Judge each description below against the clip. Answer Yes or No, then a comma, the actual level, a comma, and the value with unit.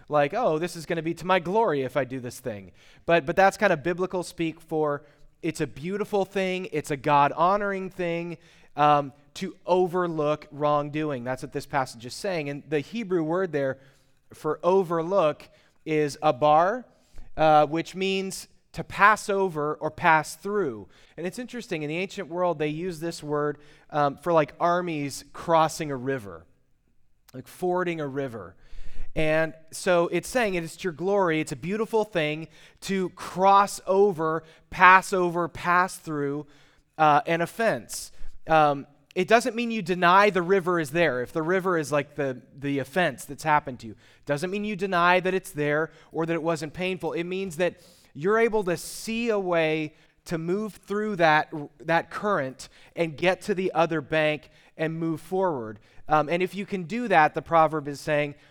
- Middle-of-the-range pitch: Yes, medium, 160 Hz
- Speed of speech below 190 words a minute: Yes, average, 180 wpm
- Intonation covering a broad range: No, average, 3.8 semitones